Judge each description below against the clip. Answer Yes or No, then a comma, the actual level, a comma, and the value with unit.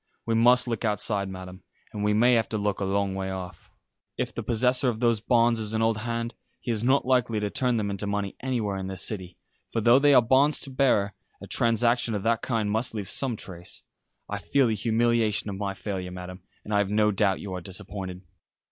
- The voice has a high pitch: No, low, 105 Hz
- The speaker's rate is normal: No, fast, 225 wpm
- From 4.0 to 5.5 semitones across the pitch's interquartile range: No, average, 3.1 semitones